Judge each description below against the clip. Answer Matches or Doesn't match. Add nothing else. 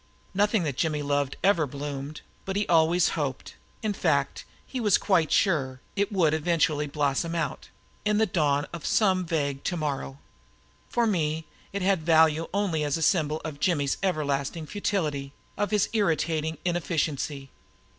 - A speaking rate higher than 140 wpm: Matches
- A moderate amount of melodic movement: Matches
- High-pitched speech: Doesn't match